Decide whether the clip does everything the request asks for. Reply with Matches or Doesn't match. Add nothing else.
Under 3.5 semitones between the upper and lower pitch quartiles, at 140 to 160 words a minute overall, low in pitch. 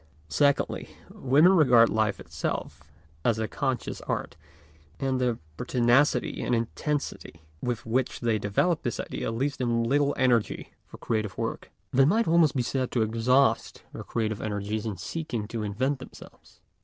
Doesn't match